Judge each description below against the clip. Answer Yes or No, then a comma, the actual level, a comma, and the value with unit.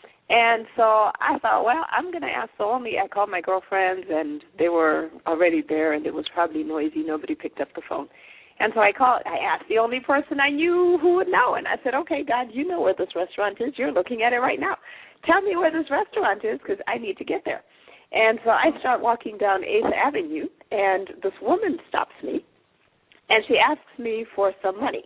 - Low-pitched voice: No, high, 235 Hz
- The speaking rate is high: Yes, fast, 225 wpm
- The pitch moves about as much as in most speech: No, wide, 9.0 semitones